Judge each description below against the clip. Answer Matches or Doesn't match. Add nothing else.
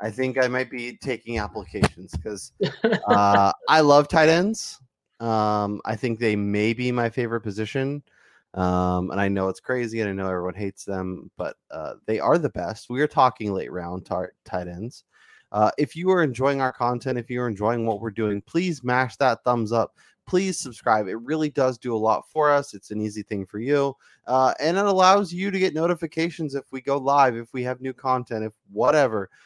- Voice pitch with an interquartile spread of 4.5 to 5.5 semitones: Matches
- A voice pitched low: Matches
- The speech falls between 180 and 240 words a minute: Matches